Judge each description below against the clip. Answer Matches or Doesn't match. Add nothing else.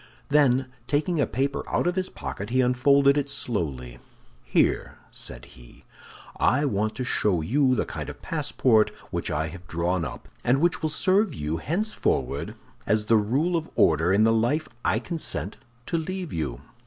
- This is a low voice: Matches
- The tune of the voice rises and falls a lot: Matches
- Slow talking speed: Doesn't match